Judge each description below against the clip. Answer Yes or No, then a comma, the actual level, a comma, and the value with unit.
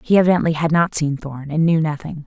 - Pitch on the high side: No, medium, 155 Hz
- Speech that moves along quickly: Yes, fast, 240 wpm